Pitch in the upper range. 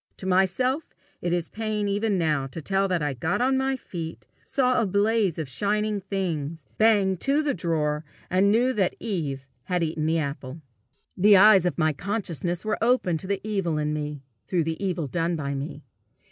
No: medium, 180 Hz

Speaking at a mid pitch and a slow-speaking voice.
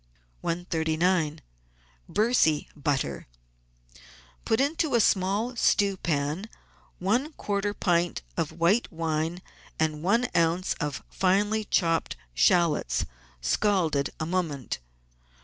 Yes: medium, 175 Hz; slow, 95 wpm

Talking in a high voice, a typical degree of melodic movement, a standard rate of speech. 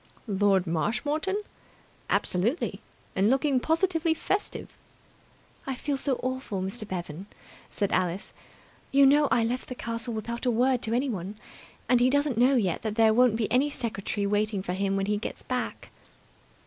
Yes: high, 235 Hz; average, 4.8 semitones; average, 160 wpm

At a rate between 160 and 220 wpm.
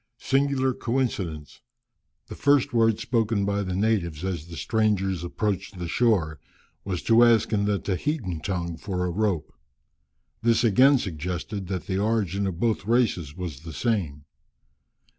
No: average, 145 wpm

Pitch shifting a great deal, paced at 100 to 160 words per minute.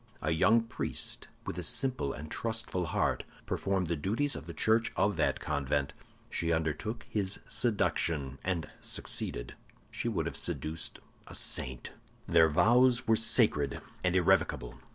Yes: wide, 6.7 semitones; average, 145 wpm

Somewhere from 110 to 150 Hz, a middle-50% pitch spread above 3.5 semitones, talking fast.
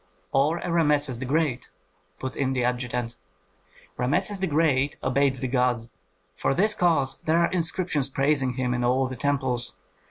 No: low, 135 Hz; average, 4.0 semitones; average, 160 wpm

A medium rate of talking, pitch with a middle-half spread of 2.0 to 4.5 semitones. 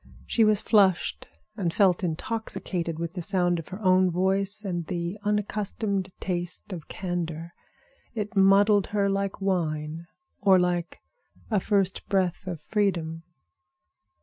No: slow, 130 wpm; average, 2.7 semitones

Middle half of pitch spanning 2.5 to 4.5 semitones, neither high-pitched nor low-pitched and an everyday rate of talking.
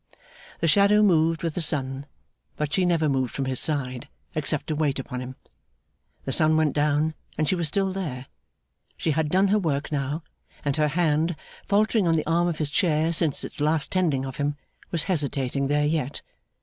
Yes: average, 2.9 semitones; medium, 155 Hz; average, 190 wpm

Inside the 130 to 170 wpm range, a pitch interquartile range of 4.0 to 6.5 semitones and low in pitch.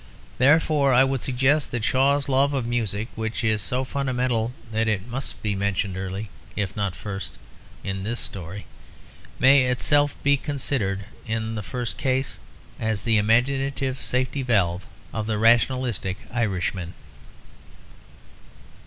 Yes: slow, 135 wpm; average, 4.5 semitones; low, 115 Hz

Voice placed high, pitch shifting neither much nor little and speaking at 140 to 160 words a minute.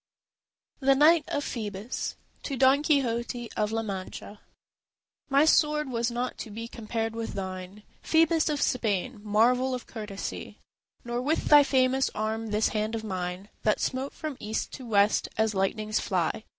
Yes: high, 230 Hz; average, 3.9 semitones; average, 155 wpm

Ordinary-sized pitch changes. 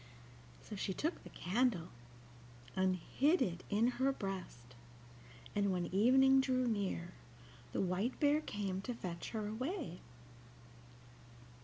No: wide, 5.8 semitones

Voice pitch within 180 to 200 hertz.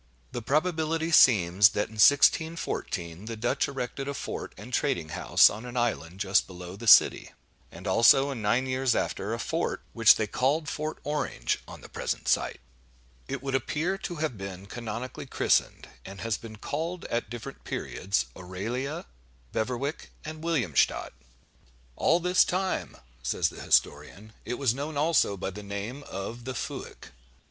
No: low, 120 Hz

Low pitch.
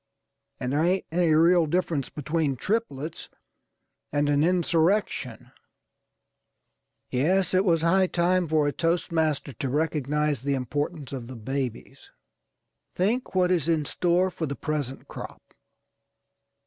No: medium, 160 Hz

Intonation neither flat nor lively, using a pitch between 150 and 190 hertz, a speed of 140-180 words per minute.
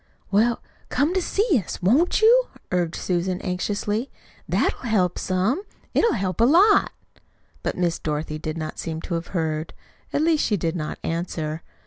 No: wide, 7.7 semitones; medium, 185 Hz; average, 160 wpm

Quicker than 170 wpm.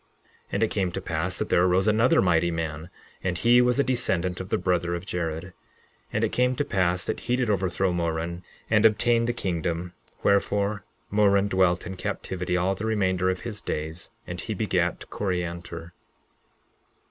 Yes: average, 180 wpm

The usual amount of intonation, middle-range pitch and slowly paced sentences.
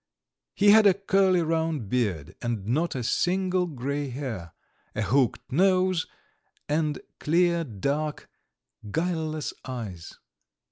No: wide, 6.4 semitones; medium, 155 Hz; slow, 110 wpm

